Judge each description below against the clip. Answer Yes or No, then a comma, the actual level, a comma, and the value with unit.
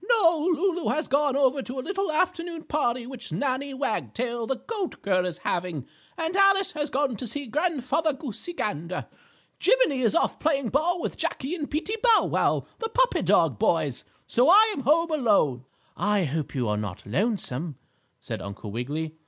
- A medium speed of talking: Yes, average, 175 wpm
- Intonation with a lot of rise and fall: Yes, wide, 8.6 semitones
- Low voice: No, very high, 275 Hz